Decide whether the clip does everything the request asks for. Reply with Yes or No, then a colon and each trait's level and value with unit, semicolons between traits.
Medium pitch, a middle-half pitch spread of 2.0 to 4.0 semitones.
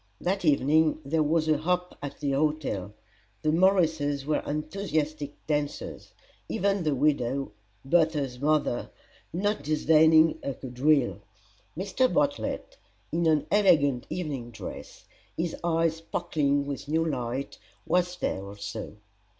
Yes: medium, 155 Hz; average, 3.0 semitones